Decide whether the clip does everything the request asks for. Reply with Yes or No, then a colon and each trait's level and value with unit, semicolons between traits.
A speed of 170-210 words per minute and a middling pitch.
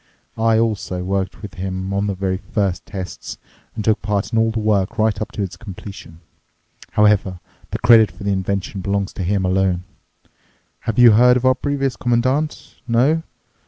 No: average, 175 wpm; low, 105 Hz